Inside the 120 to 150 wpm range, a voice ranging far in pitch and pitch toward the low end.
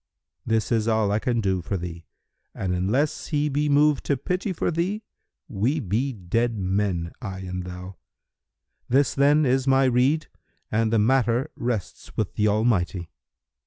No: average, 160 wpm; wide, 6.1 semitones; low, 115 Hz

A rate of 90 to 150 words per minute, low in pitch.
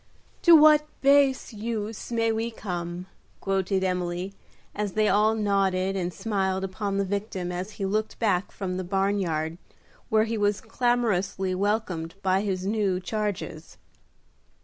No: average, 145 wpm; high, 200 Hz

